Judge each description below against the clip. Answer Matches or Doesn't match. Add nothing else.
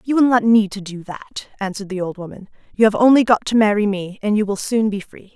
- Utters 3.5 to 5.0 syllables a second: Doesn't match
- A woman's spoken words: Matches